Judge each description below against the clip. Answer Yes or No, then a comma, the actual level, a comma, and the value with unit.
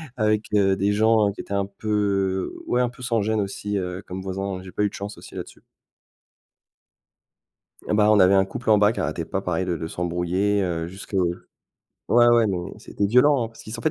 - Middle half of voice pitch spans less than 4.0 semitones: Yes, narrow, 2.4 semitones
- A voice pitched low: Yes, low, 100 Hz